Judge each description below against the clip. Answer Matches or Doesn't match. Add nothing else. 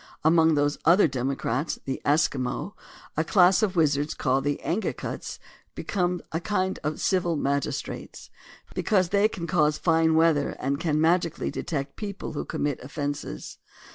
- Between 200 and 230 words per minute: Doesn't match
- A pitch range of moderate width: Matches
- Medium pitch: Matches